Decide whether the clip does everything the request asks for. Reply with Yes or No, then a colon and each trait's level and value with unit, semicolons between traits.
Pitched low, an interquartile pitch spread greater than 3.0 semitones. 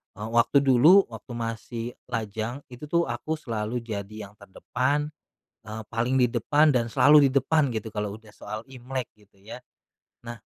Yes: low, 120 Hz; average, 3.6 semitones